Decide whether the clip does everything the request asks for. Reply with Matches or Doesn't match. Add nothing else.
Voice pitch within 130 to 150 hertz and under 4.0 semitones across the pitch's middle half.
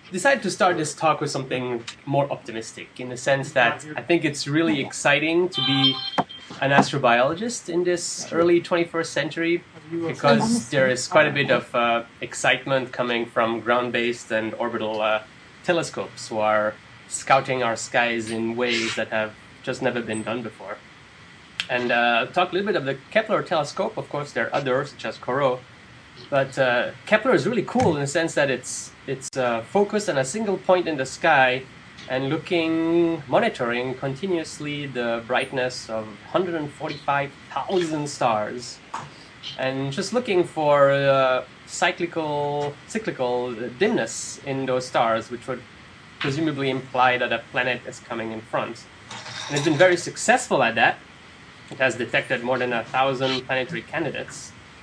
Doesn't match